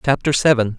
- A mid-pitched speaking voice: No, low, 130 Hz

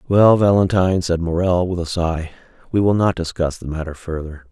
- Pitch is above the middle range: No, very low, 90 Hz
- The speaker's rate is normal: Yes, average, 185 wpm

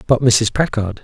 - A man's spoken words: Yes, male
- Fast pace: No, average, 175 wpm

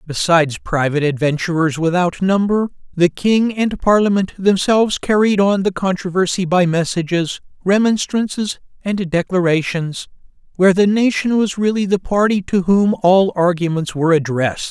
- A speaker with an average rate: No, slow, 130 wpm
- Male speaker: Yes, male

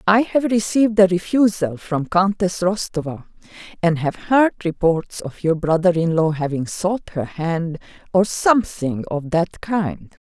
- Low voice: No, medium, 180 Hz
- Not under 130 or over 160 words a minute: Yes, average, 150 wpm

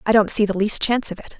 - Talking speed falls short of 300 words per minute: No, fast, 345 wpm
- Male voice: No, female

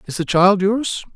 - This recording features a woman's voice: No, male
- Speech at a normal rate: No, fast, 210 wpm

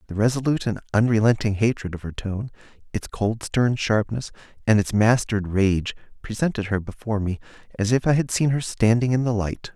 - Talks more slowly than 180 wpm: No, average, 185 wpm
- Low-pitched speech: Yes, low, 110 Hz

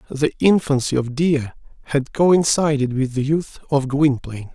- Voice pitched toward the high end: No, medium, 140 Hz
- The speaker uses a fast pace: No, average, 145 wpm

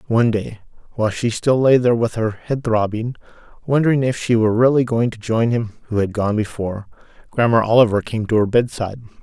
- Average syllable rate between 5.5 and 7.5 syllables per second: Yes, 6.0 syllables/s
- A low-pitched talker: Yes, low, 115 Hz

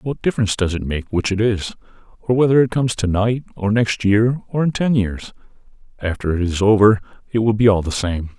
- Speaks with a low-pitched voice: Yes, low, 105 Hz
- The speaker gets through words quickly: Yes, fast, 215 wpm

